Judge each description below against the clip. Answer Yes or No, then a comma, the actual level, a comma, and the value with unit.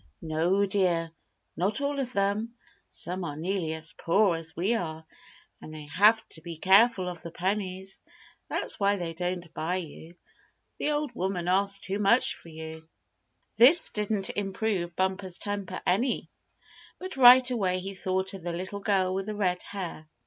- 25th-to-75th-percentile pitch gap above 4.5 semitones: No, average, 3.0 semitones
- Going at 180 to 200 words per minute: No, average, 165 wpm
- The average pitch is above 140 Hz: Yes, high, 190 Hz